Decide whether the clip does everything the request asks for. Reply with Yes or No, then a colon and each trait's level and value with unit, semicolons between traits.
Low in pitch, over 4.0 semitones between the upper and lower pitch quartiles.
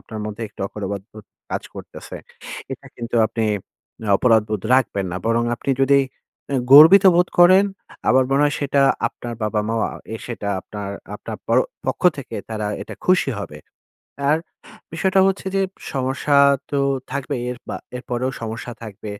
Yes: low, 120 Hz; average, 4.6 semitones